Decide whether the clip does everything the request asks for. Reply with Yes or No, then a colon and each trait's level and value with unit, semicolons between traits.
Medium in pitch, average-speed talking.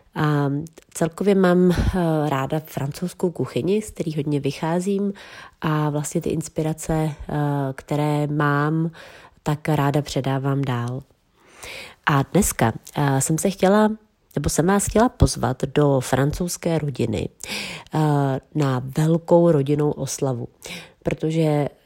No: medium, 150 Hz; slow, 105 wpm